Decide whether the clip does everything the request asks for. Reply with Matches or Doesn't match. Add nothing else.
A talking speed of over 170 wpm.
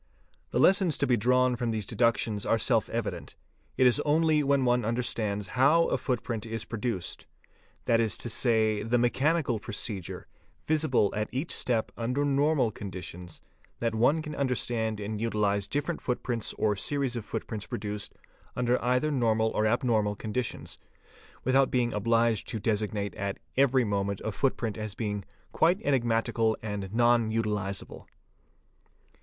Doesn't match